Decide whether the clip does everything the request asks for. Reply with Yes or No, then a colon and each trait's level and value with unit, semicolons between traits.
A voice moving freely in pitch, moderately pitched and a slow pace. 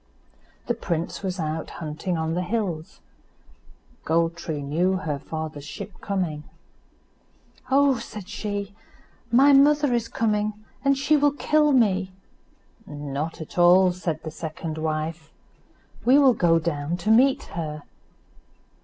Yes: wide, 6.3 semitones; medium, 180 Hz; slow, 130 wpm